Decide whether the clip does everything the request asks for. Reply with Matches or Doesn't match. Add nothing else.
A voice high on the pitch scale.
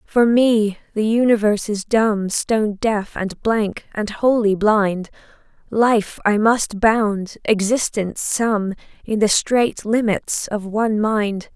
Matches